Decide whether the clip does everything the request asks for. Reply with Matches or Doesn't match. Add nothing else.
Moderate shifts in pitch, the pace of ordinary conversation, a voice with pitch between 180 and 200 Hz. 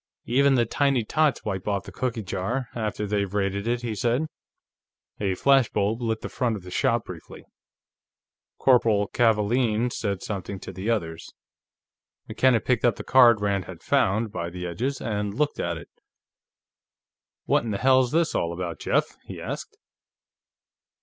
Doesn't match